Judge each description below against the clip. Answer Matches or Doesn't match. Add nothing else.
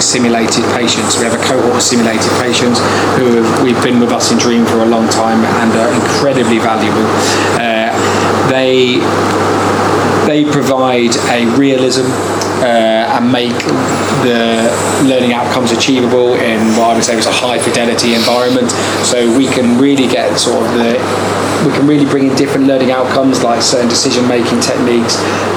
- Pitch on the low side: Matches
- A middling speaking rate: Matches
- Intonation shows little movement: Matches